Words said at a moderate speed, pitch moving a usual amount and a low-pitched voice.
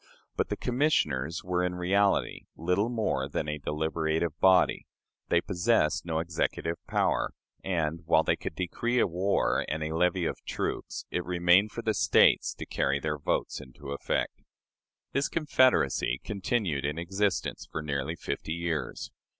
Yes: average, 150 wpm; average, 3.8 semitones; very low, 85 Hz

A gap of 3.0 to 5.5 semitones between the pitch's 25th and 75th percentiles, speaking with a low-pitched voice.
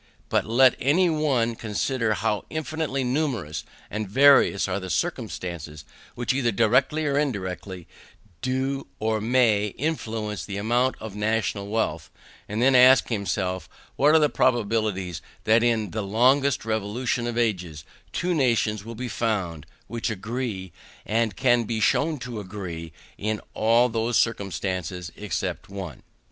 Yes: average, 4.3 semitones; low, 110 Hz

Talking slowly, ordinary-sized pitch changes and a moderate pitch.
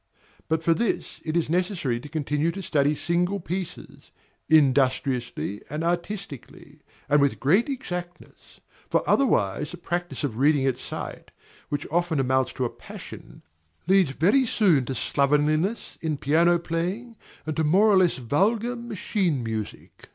No: average, 145 wpm; average, 4.8 semitones; medium, 165 Hz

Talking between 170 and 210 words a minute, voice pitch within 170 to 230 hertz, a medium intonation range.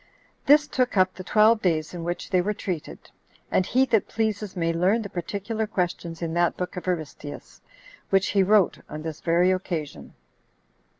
Yes: average, 175 wpm; medium, 185 Hz; average, 3.8 semitones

